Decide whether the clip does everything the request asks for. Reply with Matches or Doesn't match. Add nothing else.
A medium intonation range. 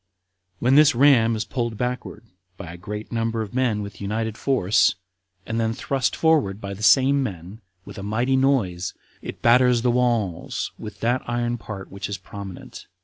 Matches